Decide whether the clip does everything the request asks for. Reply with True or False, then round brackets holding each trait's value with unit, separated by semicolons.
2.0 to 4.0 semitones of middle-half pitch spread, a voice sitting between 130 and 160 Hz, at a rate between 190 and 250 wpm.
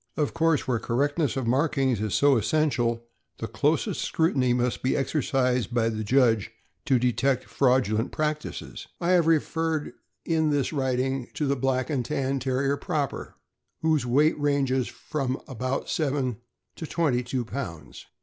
False (3.2 semitones; 135 Hz; 150 wpm)